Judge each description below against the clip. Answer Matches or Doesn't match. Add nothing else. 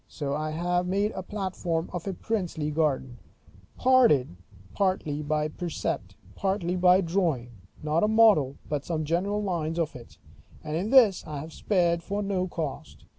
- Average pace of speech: Matches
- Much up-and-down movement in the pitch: Doesn't match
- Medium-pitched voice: Matches